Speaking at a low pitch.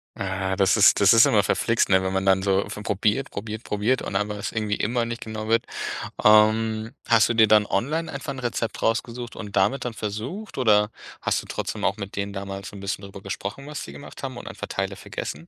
Yes: low, 105 Hz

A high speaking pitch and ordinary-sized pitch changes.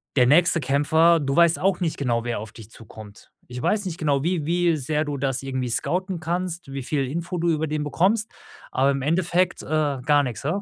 No: medium, 150 Hz; average, 4.1 semitones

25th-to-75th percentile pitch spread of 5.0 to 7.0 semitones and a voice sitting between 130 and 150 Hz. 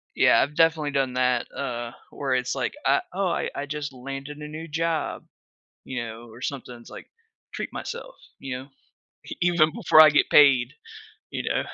No: average, 3.5 semitones; medium, 140 Hz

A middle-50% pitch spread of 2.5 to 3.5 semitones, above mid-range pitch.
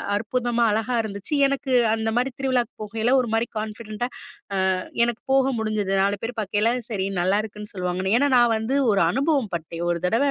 Yes: average, 3.1 semitones; high, 220 Hz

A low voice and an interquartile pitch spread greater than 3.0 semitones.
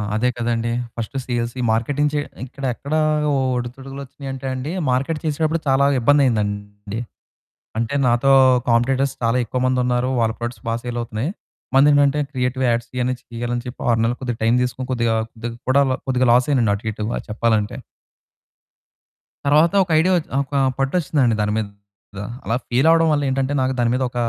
No: low, 125 Hz; average, 2.7 semitones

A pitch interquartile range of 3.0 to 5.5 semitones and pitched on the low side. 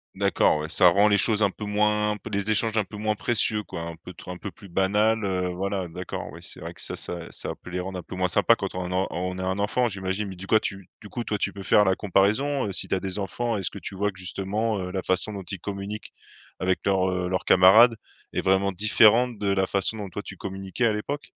No: narrow, 2.4 semitones; low, 100 Hz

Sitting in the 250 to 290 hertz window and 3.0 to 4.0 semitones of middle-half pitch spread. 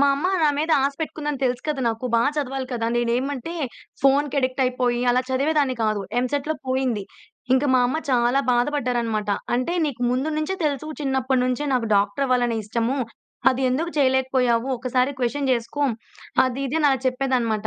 No: very high, 255 Hz; narrow, 2.5 semitones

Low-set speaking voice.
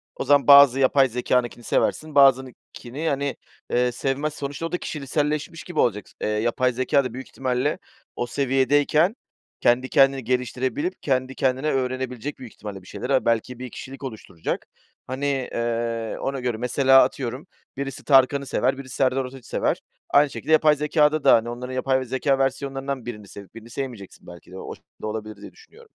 Yes: low, 130 Hz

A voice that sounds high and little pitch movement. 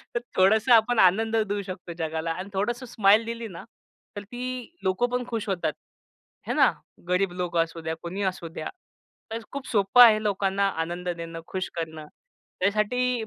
No: high, 195 Hz; average, 4.2 semitones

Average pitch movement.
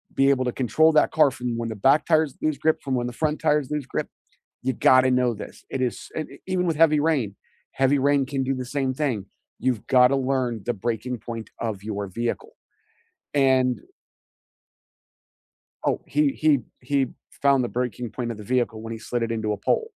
Yes: average, 3.4 semitones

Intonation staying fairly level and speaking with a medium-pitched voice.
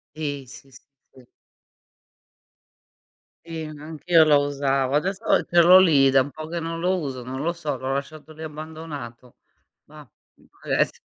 No: average, 3.1 semitones; medium, 150 Hz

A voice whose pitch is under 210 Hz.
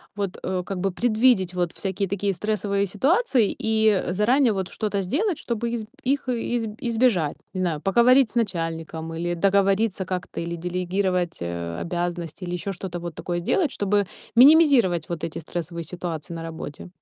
Yes: high, 190 Hz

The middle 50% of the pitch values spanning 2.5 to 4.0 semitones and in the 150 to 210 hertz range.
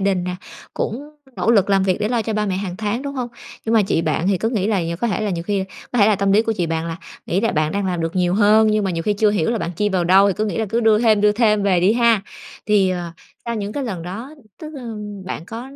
Yes: average, 3.3 semitones; high, 205 Hz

